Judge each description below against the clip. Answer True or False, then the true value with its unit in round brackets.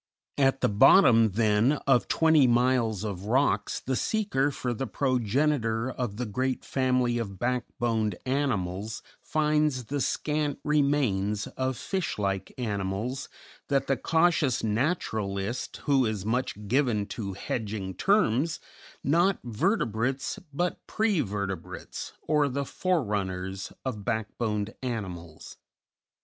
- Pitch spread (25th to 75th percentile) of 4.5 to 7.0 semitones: True (5.1 semitones)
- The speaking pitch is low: True (125 Hz)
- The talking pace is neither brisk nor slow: False (115 wpm)